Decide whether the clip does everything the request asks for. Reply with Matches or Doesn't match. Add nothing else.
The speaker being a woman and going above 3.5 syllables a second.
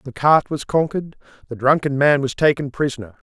Doesn't match